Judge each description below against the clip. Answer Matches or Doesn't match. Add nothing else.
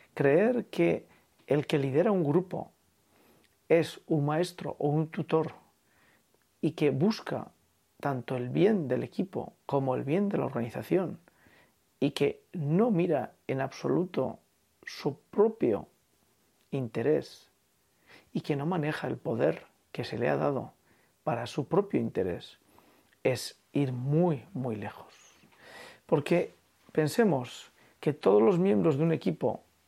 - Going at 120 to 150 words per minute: Matches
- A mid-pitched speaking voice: Matches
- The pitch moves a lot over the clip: Doesn't match